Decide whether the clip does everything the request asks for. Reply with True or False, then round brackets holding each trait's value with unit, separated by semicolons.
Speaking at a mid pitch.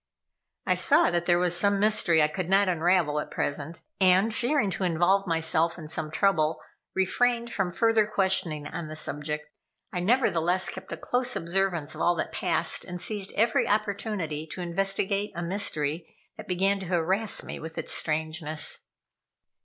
True (180 Hz)